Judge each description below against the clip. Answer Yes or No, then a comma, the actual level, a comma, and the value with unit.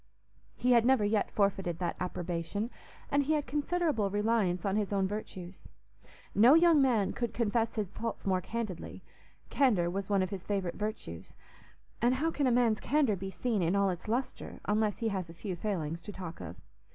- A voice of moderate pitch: No, high, 210 Hz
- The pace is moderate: Yes, average, 190 wpm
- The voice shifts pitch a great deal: No, average, 4.3 semitones